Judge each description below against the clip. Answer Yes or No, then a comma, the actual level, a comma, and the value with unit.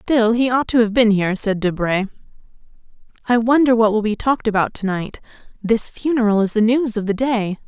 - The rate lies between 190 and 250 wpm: Yes, fast, 205 wpm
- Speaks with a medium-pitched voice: No, high, 220 Hz